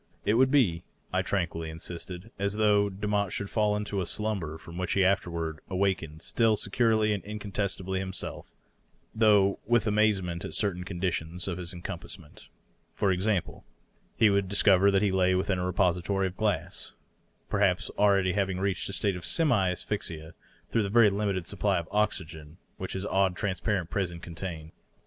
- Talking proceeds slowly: No, average, 165 wpm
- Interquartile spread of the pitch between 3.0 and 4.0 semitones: No, narrow, 2.6 semitones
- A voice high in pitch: No, very low, 95 Hz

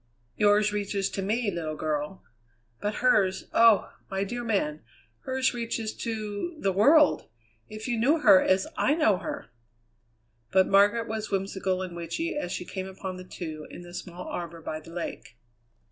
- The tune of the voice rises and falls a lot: No, average, 3.9 semitones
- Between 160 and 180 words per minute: Yes, average, 165 wpm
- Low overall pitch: No, high, 195 Hz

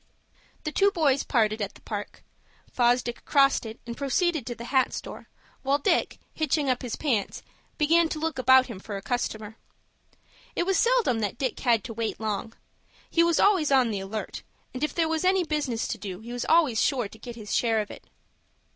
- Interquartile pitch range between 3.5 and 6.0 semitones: Yes, wide, 5.5 semitones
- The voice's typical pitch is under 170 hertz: No, very high, 250 Hz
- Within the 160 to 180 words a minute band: No, average, 200 wpm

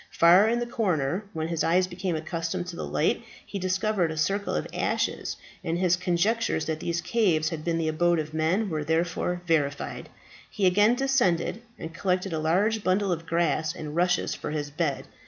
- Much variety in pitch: No, average, 3.2 semitones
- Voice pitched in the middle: Yes, medium, 175 Hz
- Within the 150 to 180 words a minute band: No, average, 190 wpm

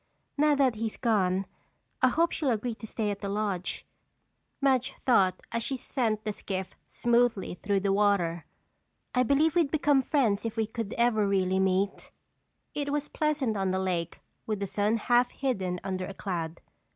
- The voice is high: Yes, high, 215 Hz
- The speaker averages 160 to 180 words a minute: Yes, average, 175 wpm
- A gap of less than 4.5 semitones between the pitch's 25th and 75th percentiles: No, average, 4.8 semitones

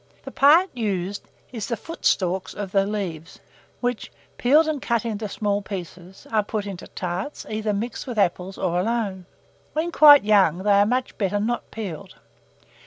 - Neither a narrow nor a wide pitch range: Yes, average, 3.9 semitones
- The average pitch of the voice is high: Yes, high, 205 Hz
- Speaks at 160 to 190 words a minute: Yes, average, 165 wpm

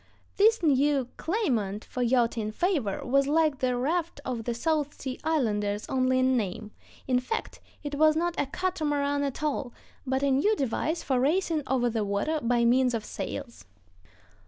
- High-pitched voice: Yes, very high, 270 Hz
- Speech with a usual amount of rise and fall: Yes, average, 4.2 semitones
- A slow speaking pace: No, average, 165 wpm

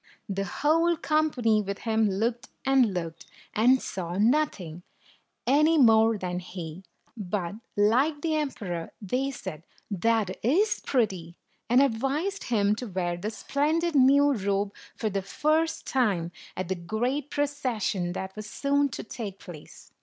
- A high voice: Yes, high, 225 Hz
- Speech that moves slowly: No, average, 150 wpm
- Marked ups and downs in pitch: Yes, wide, 6.6 semitones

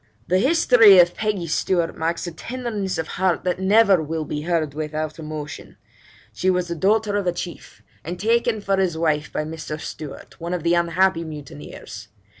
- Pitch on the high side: No, medium, 175 Hz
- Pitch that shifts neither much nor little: Yes, average, 3.5 semitones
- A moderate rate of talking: Yes, average, 180 wpm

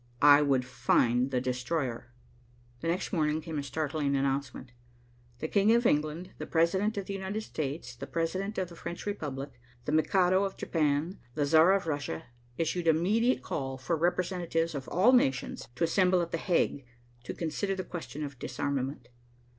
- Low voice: No, medium, 160 Hz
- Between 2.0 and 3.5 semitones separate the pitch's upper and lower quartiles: No, average, 4.7 semitones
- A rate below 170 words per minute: No, average, 175 wpm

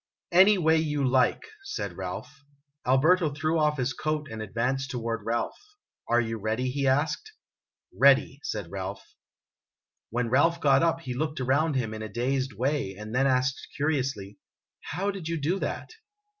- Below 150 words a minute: No, average, 170 wpm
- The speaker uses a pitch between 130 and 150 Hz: Yes, low, 135 Hz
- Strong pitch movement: No, average, 4.6 semitones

